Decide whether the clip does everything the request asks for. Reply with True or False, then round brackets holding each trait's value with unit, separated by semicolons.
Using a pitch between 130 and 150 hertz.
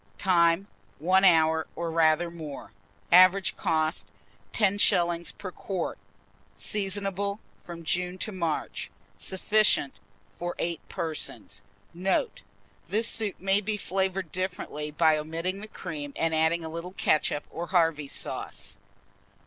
False (175 Hz)